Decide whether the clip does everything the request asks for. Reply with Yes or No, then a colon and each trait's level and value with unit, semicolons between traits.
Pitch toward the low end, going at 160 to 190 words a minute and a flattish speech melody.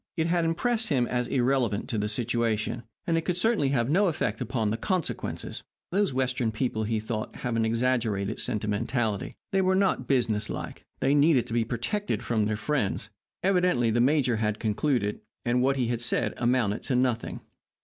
No: low, 120 Hz; average, 180 wpm; average, 4.7 semitones